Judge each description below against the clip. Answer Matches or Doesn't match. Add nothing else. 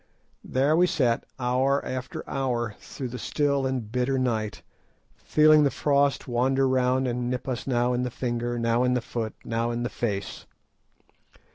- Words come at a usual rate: Matches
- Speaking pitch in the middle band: Doesn't match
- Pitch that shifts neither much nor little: Doesn't match